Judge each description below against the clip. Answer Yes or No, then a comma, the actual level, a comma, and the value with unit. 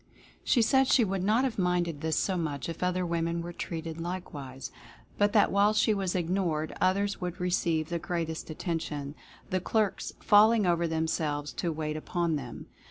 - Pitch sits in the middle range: Yes, medium, 175 Hz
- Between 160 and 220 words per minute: Yes, average, 170 wpm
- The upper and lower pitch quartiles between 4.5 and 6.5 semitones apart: No, average, 3.3 semitones